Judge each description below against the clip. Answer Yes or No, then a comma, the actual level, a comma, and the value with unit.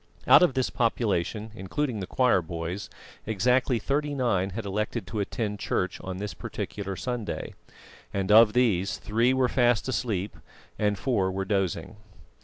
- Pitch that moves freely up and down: No, average, 4.2 semitones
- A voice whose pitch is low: Yes, low, 105 Hz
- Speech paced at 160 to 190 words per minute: No, average, 150 wpm